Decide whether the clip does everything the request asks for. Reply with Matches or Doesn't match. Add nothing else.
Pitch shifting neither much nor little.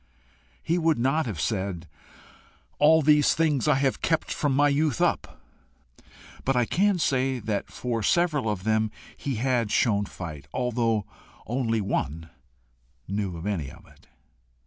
Doesn't match